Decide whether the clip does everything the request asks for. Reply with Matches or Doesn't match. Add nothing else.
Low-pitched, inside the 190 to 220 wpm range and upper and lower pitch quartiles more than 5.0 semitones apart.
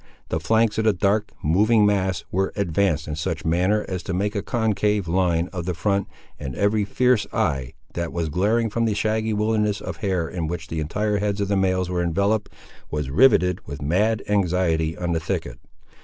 Doesn't match